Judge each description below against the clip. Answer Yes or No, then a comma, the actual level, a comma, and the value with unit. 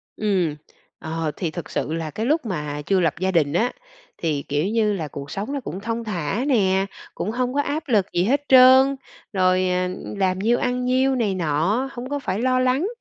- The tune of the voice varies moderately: No, wide, 6.6 semitones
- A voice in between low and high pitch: No, high, 200 Hz